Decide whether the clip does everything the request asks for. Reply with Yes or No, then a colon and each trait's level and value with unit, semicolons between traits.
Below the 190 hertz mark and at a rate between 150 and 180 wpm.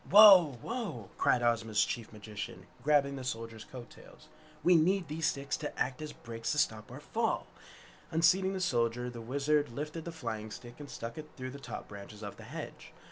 No: low, 135 Hz; average, 190 wpm